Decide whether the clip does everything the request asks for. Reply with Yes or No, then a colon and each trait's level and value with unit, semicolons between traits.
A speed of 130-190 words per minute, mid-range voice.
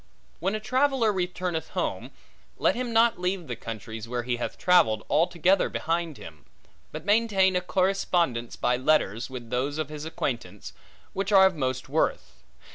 Yes: average, 160 wpm; medium, 160 Hz